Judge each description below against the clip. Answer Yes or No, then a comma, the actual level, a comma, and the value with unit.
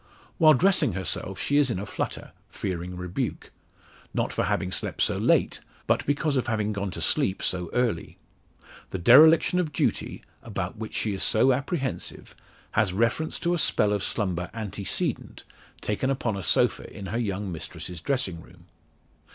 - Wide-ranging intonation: Yes, wide, 6.2 semitones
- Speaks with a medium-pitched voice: No, low, 105 Hz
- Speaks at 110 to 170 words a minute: Yes, average, 165 wpm